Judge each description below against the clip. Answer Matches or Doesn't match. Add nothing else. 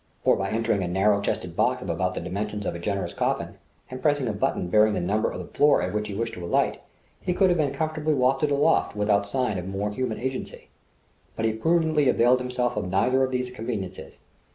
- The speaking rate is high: Matches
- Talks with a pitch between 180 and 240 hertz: Doesn't match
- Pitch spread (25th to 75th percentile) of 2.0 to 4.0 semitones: Doesn't match